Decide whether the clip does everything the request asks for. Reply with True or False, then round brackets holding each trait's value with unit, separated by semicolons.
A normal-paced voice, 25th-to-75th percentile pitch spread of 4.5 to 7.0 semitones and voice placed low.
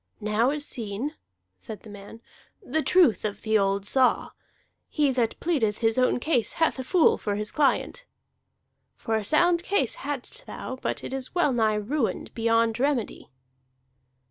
False (160 wpm; 5.3 semitones; 245 Hz)